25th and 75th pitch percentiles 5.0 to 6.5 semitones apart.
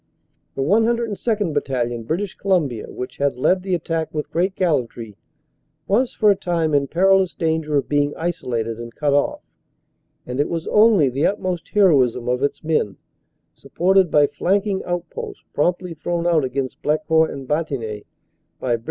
Yes: wide, 5.4 semitones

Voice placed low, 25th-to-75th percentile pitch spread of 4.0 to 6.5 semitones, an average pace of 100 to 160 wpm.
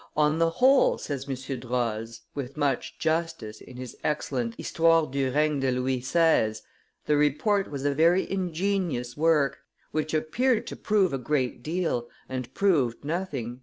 No: medium, 145 Hz; average, 4.5 semitones; average, 155 wpm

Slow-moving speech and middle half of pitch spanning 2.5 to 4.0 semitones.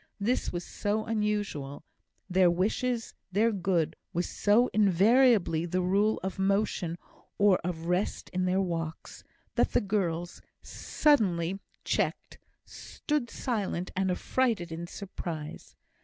Yes: slow, 120 wpm; average, 3.6 semitones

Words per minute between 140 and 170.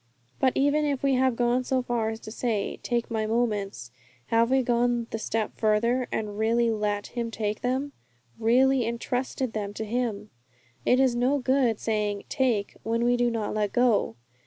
No: average, 180 wpm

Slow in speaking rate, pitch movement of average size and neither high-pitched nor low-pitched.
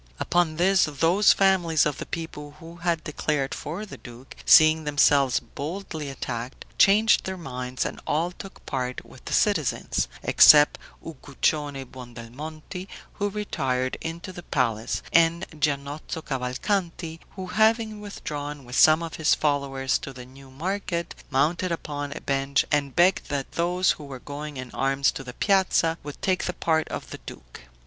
No: average, 155 wpm; average, 4.3 semitones; medium, 150 Hz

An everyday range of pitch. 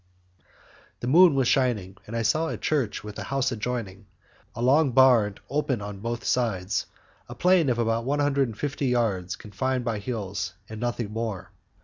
Yes: average, 4.1 semitones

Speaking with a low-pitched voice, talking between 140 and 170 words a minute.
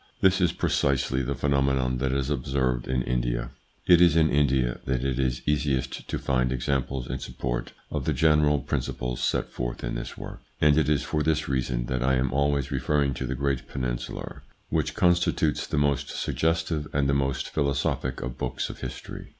No: very low, 65 Hz; average, 185 wpm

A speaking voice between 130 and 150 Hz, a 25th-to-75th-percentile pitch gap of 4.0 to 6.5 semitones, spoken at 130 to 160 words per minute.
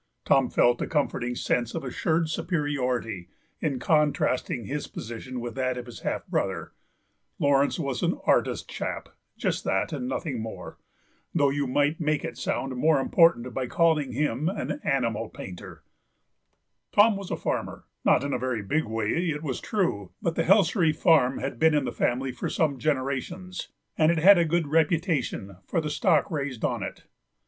No: medium, 140 Hz; average, 4.5 semitones; average, 175 wpm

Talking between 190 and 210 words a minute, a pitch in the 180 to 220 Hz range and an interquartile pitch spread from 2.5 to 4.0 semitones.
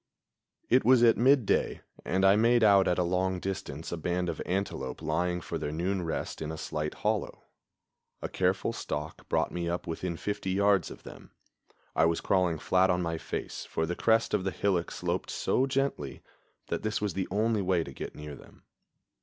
No: average, 195 wpm; very low, 90 Hz; average, 3.6 semitones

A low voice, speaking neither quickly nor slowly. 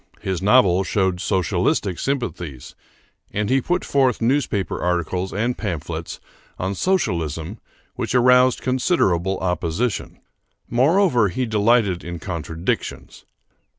No: low, 100 Hz; slow, 105 wpm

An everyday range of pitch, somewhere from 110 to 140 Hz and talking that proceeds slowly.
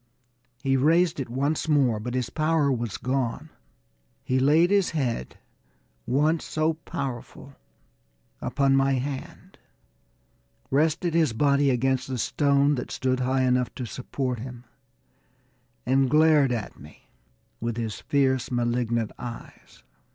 Yes: average, 3.1 semitones; low, 135 Hz; slow, 125 wpm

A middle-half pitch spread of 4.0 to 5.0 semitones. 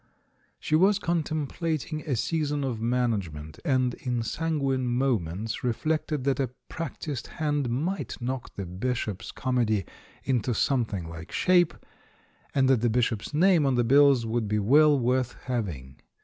Yes: average, 4.7 semitones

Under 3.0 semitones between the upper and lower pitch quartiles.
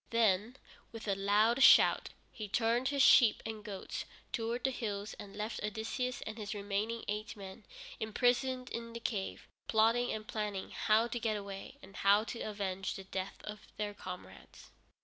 Yes: narrow, 2.4 semitones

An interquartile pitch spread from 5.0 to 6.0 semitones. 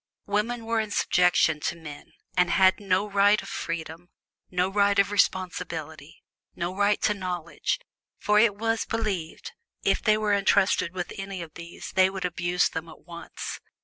No: average, 3.1 semitones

